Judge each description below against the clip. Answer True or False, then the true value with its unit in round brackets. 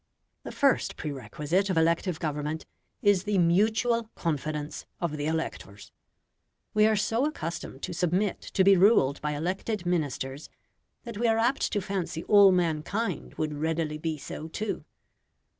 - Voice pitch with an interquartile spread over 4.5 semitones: True (5.0 semitones)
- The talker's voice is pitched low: False (175 Hz)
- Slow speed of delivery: False (145 wpm)